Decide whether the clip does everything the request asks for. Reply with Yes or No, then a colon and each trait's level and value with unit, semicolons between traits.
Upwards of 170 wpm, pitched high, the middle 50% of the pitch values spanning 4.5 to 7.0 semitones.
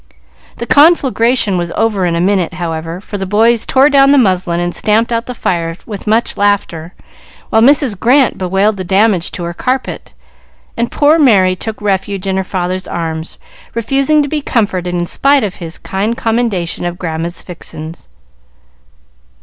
No: average, 165 wpm; high, 200 Hz; average, 5.0 semitones